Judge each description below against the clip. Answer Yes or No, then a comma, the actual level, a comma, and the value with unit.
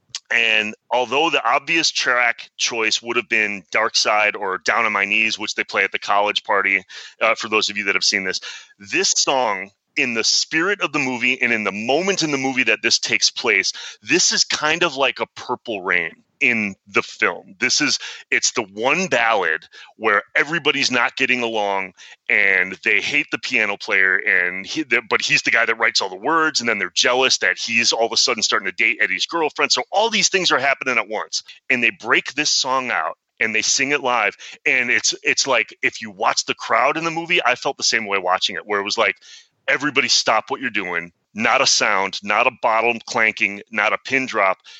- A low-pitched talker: Yes, low, 120 Hz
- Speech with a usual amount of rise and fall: No, wide, 5.8 semitones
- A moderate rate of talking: No, fast, 220 wpm